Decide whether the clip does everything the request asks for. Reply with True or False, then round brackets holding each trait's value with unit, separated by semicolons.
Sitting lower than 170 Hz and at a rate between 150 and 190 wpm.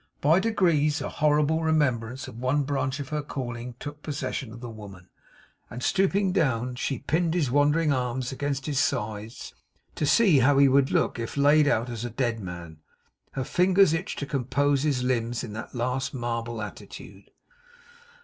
True (135 Hz; 170 wpm)